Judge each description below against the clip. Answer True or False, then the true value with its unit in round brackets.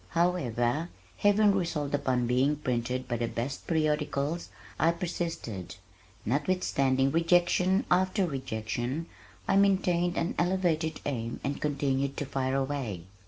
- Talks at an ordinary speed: False (115 wpm)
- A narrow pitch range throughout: False (5.0 semitones)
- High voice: False (145 Hz)